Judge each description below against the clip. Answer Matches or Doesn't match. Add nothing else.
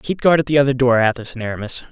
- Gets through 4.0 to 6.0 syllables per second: Doesn't match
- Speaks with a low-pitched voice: Matches